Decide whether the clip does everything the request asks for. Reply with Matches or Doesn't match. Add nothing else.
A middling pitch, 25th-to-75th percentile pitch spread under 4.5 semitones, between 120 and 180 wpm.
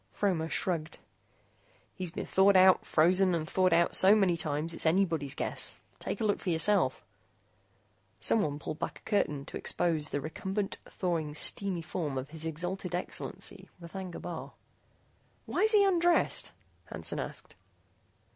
Matches